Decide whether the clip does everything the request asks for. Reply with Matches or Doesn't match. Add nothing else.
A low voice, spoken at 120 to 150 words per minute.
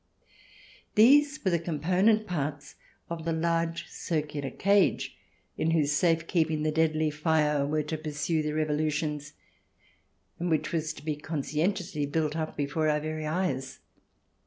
Doesn't match